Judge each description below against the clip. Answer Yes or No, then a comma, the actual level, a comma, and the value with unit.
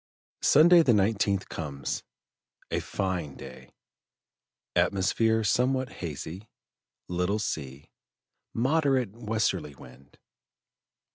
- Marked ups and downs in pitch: Yes, wide, 7.0 semitones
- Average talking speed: No, slow, 80 wpm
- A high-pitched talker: No, low, 100 Hz